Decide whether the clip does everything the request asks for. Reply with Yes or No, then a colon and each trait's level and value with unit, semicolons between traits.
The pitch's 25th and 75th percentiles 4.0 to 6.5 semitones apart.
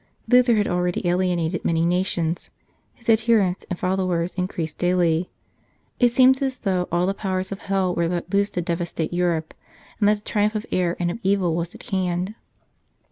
No: narrow, 2.6 semitones